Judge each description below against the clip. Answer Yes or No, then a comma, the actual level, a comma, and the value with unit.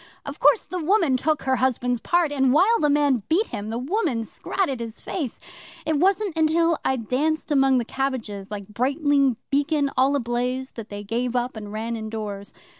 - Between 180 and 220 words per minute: Yes, average, 185 wpm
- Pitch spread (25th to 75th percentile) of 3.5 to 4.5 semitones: No, average, 5.0 semitones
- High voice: Yes, very high, 265 Hz